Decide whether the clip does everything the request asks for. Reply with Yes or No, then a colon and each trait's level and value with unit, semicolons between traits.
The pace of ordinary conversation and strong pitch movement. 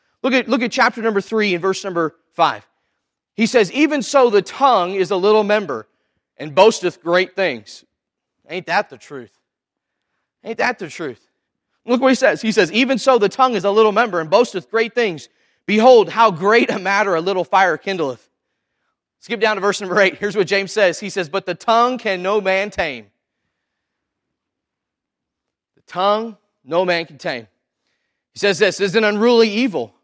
No: average, 185 wpm; average, 3.8 semitones